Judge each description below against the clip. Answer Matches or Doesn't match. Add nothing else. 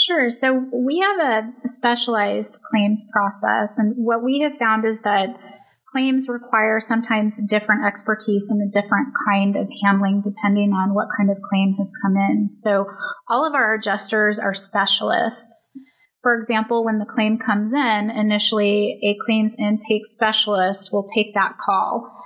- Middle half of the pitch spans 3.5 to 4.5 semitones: Doesn't match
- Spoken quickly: Doesn't match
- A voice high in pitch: Matches